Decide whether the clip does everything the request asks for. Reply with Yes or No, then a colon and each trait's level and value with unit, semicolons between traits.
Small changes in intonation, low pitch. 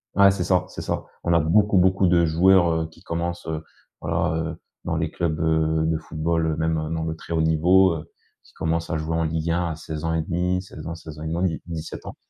Yes: narrow, 1.5 semitones; very low, 80 Hz